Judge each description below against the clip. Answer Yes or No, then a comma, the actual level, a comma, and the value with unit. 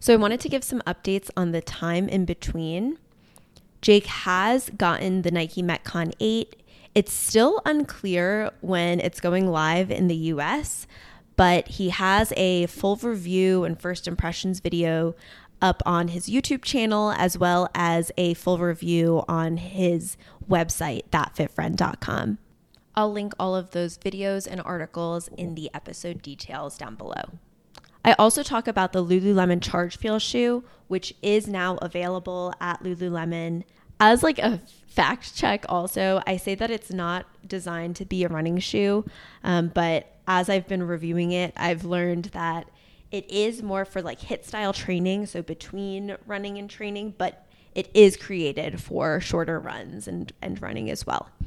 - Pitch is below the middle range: No, medium, 180 Hz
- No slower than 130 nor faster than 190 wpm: Yes, average, 155 wpm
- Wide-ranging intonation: No, average, 2.7 semitones